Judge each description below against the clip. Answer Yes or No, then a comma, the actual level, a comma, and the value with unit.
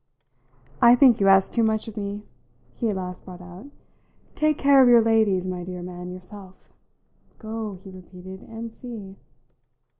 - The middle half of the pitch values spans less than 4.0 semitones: Yes, average, 3.6 semitones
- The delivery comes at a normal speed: Yes, average, 160 wpm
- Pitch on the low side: No, high, 200 Hz